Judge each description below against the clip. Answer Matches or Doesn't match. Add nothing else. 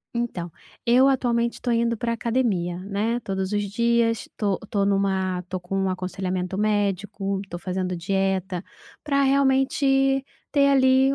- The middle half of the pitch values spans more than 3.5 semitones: Matches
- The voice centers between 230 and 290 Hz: Doesn't match